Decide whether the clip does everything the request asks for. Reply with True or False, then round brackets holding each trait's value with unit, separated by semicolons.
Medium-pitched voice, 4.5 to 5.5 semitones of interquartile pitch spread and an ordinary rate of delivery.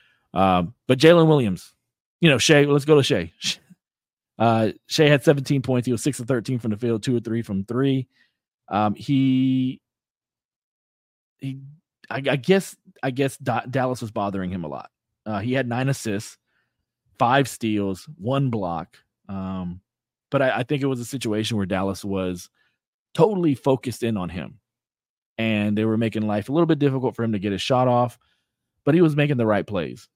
False (125 Hz; 4.9 semitones; 185 wpm)